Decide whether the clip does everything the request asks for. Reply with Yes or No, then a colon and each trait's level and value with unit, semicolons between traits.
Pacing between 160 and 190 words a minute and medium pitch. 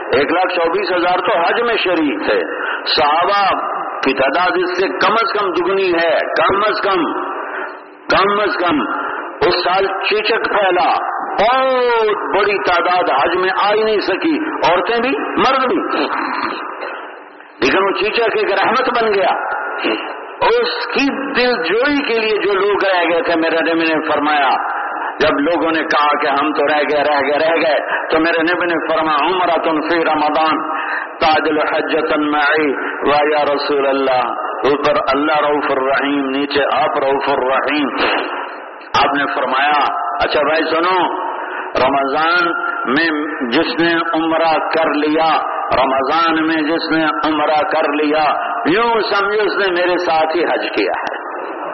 No: average, 145 wpm; medium, 165 Hz